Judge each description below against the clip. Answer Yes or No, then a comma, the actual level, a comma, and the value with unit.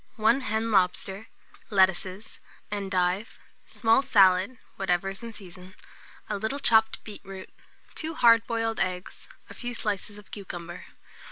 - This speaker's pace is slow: Yes, slow, 125 wpm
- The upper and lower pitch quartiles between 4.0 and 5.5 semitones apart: No, average, 3.2 semitones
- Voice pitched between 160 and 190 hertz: No, high, 205 Hz